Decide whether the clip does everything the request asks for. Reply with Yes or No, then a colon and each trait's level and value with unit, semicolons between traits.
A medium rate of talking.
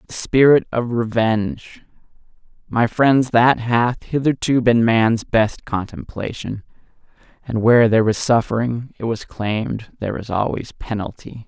No: slow, 130 wpm